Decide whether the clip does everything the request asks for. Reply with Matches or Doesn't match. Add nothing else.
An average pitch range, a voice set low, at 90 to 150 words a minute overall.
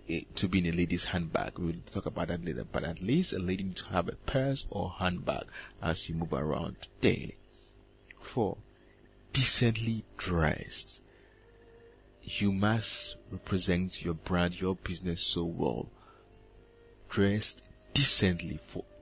Matches